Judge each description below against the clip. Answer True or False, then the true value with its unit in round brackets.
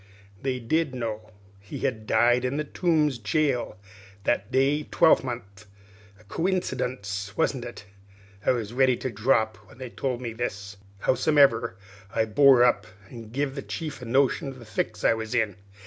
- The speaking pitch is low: True (125 Hz)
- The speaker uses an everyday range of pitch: True (3.8 semitones)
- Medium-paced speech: True (165 wpm)